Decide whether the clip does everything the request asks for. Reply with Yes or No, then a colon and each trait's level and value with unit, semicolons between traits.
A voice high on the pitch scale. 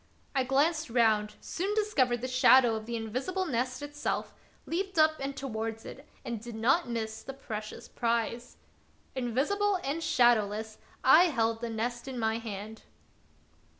Yes: high, 245 Hz